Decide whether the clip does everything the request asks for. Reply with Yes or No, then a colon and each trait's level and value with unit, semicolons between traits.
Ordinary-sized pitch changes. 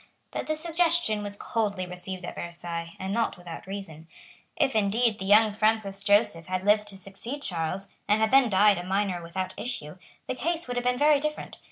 Yes: average, 4.8 semitones